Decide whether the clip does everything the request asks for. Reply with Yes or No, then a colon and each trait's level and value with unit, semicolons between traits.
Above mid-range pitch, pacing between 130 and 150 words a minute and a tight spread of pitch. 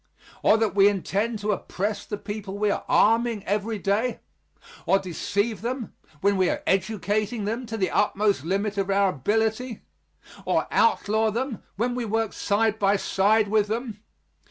No: high, 210 Hz; average, 160 wpm; narrow, 2.0 semitones